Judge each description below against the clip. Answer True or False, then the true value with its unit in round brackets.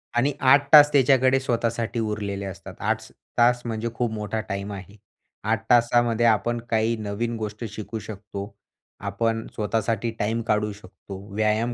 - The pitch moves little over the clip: True (2.3 semitones)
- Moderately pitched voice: False (110 Hz)